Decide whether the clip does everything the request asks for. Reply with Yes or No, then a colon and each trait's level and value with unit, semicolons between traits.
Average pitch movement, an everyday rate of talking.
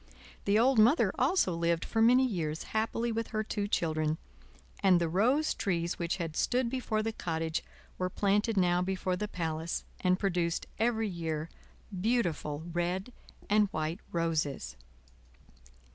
Yes: average, 4.8 semitones; average, 145 wpm